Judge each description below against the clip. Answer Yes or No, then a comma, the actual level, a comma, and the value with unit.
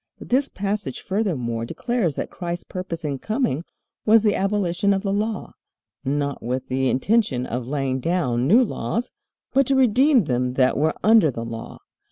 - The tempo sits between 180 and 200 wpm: No, average, 165 wpm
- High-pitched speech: No, medium, 175 Hz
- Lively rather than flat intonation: Yes, wide, 8.6 semitones